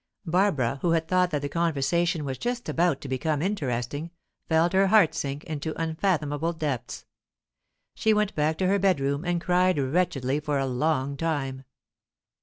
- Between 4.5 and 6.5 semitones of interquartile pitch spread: No, average, 4.1 semitones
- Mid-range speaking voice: Yes, medium, 160 Hz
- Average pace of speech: Yes, average, 160 wpm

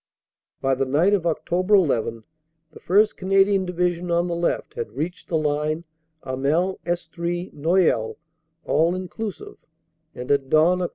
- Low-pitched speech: No, medium, 170 Hz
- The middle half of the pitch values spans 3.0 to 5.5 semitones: Yes, average, 3.4 semitones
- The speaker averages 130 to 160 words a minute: Yes, average, 155 wpm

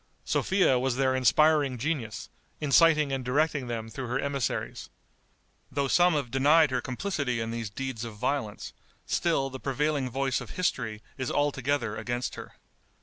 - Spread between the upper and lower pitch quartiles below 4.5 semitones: Yes, average, 3.1 semitones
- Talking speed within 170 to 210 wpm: No, average, 150 wpm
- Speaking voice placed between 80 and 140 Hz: Yes, low, 135 Hz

